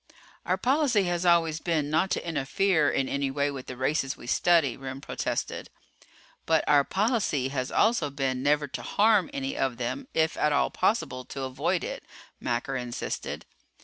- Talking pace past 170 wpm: No, average, 165 wpm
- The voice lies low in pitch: No, medium, 150 Hz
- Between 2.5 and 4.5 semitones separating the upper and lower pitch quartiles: No, average, 5.2 semitones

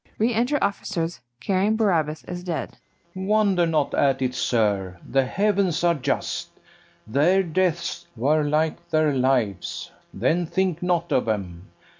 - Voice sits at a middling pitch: Yes, medium, 165 Hz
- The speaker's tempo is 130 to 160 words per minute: Yes, average, 140 wpm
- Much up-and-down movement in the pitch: Yes, wide, 5.8 semitones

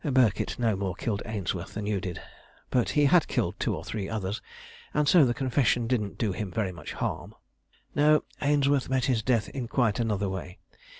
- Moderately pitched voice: No, low, 115 Hz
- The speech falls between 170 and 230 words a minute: Yes, average, 190 wpm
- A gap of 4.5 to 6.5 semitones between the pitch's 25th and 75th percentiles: Yes, average, 4.8 semitones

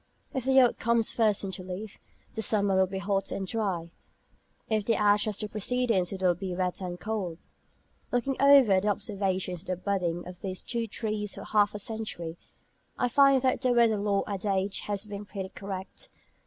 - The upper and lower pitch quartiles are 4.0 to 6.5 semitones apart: No, average, 2.8 semitones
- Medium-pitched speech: No, high, 205 Hz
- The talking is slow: No, average, 190 wpm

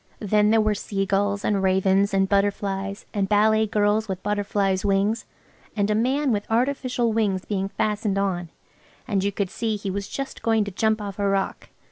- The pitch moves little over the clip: Yes, narrow, 1.7 semitones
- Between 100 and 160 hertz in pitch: No, high, 205 Hz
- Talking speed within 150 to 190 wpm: Yes, average, 180 wpm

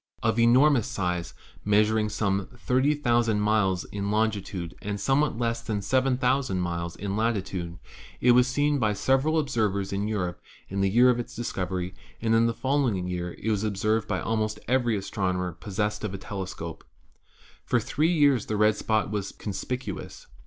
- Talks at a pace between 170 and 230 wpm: No, average, 160 wpm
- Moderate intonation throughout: Yes, average, 3.8 semitones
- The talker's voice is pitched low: Yes, low, 105 Hz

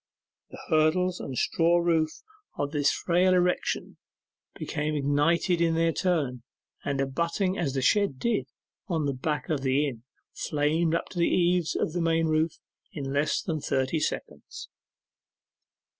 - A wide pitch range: No, average, 3.1 semitones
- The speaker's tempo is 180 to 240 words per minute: No, average, 150 wpm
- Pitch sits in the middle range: Yes, medium, 160 Hz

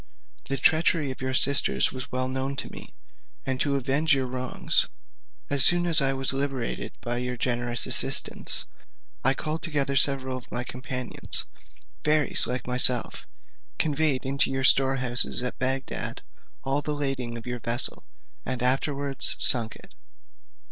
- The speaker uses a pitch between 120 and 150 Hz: Yes, low, 135 Hz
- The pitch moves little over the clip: Yes, narrow, 1.8 semitones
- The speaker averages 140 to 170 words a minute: Yes, average, 150 wpm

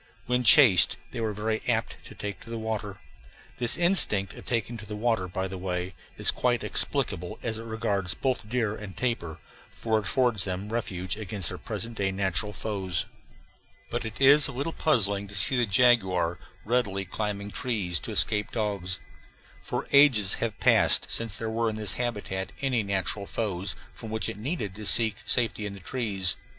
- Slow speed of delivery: No, average, 180 wpm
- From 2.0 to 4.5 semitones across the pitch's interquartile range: Yes, average, 3.3 semitones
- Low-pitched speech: Yes, low, 105 Hz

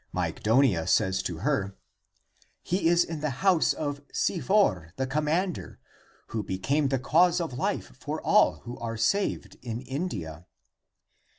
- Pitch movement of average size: No, wide, 7.8 semitones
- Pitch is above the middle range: No, low, 135 Hz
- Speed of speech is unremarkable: Yes, average, 150 wpm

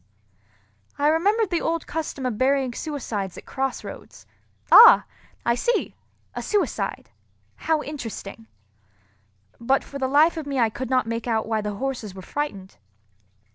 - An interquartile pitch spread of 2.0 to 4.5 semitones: No, average, 5.2 semitones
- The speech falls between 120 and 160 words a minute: Yes, average, 150 wpm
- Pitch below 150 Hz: No, very high, 265 Hz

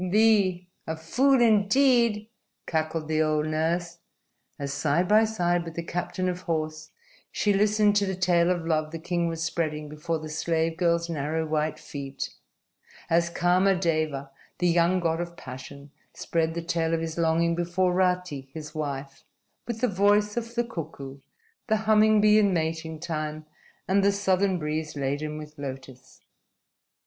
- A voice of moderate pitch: Yes, medium, 170 Hz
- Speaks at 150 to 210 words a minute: Yes, average, 160 wpm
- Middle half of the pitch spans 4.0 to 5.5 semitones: No, average, 3.3 semitones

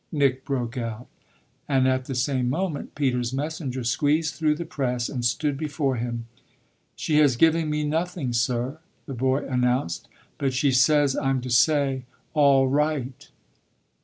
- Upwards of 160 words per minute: No, average, 150 wpm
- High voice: No, low, 135 Hz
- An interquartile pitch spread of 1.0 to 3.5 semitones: Yes, average, 3.1 semitones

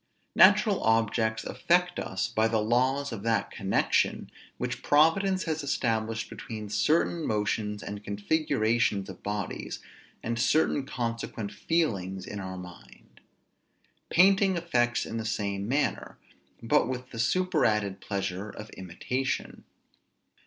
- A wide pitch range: Yes, wide, 6.2 semitones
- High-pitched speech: No, low, 115 Hz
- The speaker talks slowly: Yes, slow, 120 wpm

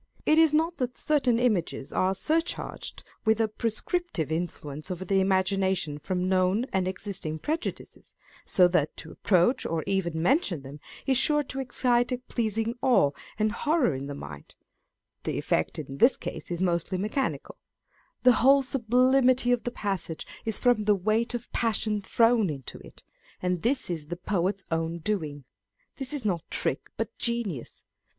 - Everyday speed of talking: Yes, average, 165 wpm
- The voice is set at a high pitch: Yes, high, 205 Hz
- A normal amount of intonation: No, wide, 6.1 semitones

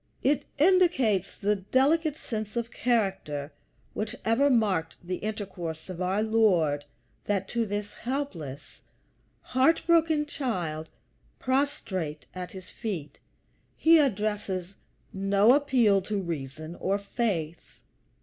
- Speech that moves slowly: Yes, slow, 110 wpm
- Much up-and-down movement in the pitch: Yes, wide, 6.1 semitones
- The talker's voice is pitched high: Yes, high, 205 Hz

